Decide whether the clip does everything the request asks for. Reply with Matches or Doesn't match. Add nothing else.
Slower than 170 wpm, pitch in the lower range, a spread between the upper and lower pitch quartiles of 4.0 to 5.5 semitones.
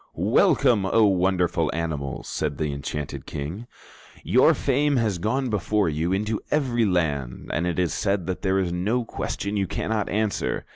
Matches